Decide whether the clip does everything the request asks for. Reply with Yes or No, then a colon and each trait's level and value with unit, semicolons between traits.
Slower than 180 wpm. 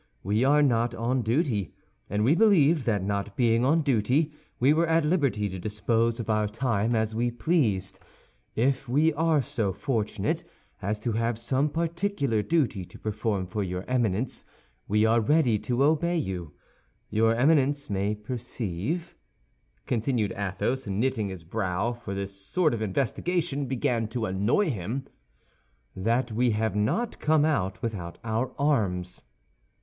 Yes: average, 150 wpm